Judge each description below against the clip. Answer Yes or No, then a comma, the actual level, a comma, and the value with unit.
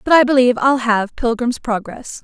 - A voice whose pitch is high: Yes, high, 245 Hz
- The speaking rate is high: No, average, 190 wpm